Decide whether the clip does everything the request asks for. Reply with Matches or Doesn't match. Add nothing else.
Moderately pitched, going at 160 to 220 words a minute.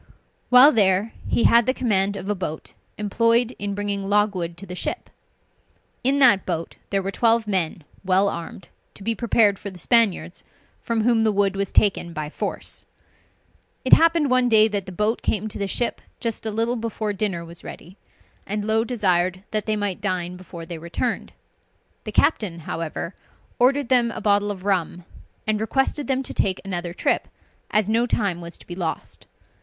Doesn't match